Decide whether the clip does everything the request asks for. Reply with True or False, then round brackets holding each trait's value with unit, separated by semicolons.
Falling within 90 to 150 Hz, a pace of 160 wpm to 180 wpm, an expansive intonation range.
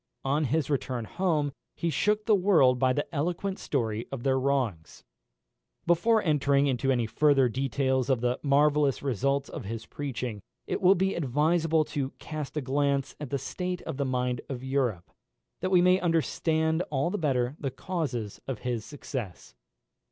False (140 Hz; 165 wpm; 3.9 semitones)